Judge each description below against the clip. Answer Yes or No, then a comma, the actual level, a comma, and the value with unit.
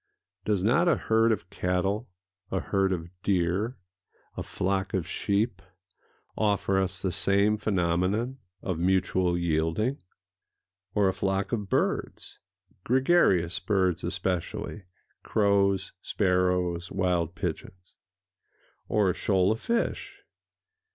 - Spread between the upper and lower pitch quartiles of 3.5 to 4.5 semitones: No, narrow, 2.5 semitones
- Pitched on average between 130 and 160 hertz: No, very low, 95 Hz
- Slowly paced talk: Yes, slow, 110 wpm